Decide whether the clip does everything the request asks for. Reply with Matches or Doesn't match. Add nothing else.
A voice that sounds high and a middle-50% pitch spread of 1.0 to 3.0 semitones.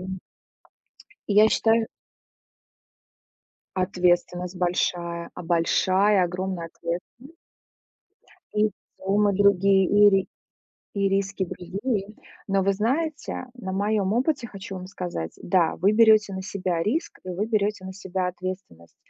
Matches